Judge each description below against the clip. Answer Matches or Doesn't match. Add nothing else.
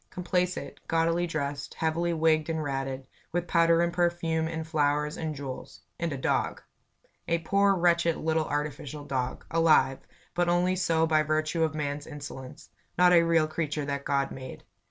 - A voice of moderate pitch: Matches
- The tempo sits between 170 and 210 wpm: Doesn't match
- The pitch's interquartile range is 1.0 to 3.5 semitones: Matches